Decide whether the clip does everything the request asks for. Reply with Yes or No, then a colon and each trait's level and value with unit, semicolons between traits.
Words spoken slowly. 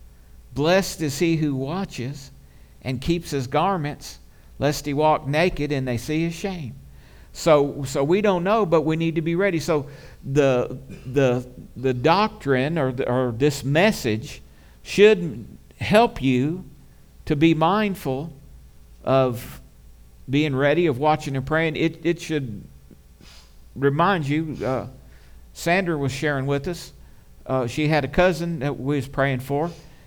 No: average, 145 wpm